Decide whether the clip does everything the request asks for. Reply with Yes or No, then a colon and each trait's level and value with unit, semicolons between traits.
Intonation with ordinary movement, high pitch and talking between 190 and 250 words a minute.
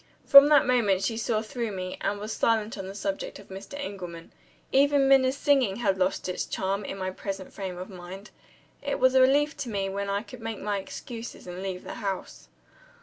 Yes: average, 4.7 semitones; high, 205 Hz; fast, 205 wpm